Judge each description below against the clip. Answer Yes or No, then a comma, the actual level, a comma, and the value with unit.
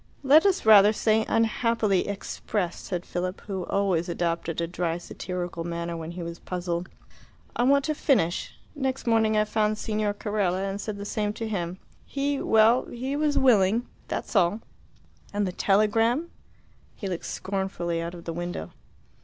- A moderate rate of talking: Yes, average, 160 wpm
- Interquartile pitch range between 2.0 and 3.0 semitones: No, average, 4.2 semitones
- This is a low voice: No, high, 200 Hz